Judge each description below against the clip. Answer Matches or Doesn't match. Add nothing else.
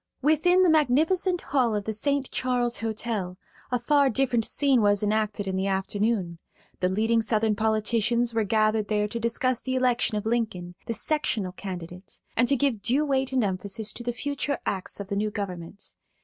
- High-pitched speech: Matches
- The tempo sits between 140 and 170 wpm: Doesn't match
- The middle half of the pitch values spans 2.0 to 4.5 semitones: Matches